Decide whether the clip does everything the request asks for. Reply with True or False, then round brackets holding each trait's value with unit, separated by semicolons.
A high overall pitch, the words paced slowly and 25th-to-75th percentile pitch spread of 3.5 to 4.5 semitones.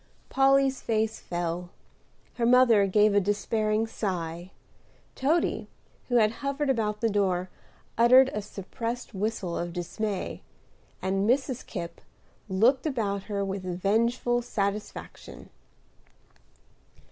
True (215 Hz; 110 wpm; 3.9 semitones)